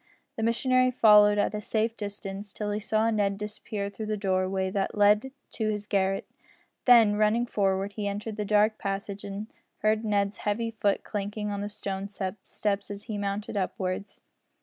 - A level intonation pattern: Yes, narrow, 1.3 semitones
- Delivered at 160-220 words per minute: Yes, average, 170 wpm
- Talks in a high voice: Yes, high, 205 Hz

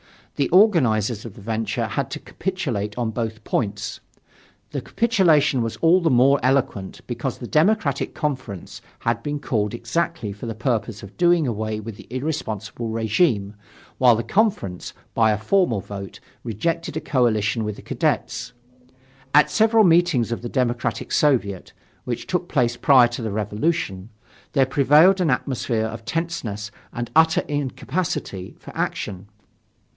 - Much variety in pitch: Yes, wide, 6.4 semitones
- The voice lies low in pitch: Yes, low, 120 Hz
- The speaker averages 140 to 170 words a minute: Yes, average, 150 wpm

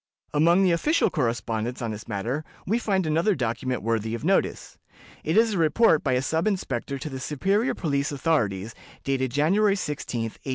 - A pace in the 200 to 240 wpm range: No, average, 175 wpm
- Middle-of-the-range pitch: Yes, medium, 145 Hz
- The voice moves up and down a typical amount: No, wide, 7.4 semitones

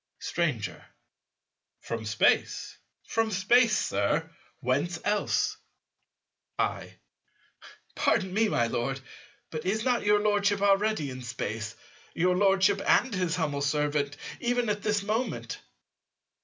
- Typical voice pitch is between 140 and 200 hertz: Yes, high, 190 Hz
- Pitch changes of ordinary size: No, wide, 6.6 semitones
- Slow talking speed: Yes, slow, 115 wpm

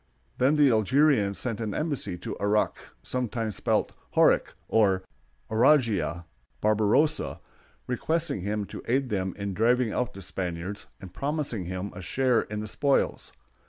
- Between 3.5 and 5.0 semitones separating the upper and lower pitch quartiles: Yes, average, 4.7 semitones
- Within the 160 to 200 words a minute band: No, average, 140 wpm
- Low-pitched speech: Yes, low, 110 Hz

